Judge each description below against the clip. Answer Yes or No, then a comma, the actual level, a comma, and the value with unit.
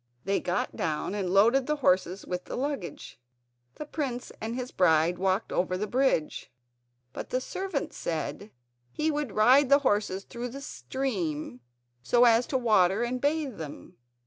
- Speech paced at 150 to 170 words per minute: Yes, average, 160 wpm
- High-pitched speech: Yes, high, 225 Hz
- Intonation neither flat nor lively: No, wide, 6.5 semitones